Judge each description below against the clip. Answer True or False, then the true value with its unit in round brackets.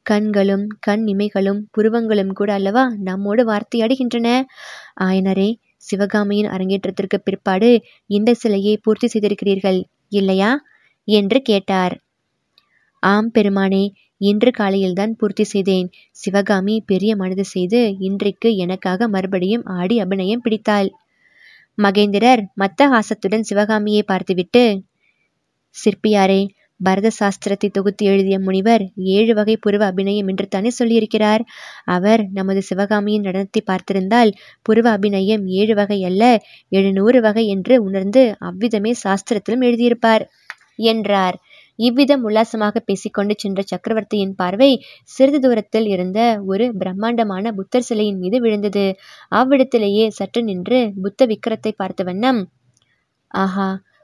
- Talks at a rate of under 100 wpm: False (105 wpm)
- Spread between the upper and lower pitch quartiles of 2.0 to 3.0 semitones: True (2.6 semitones)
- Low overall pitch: False (205 Hz)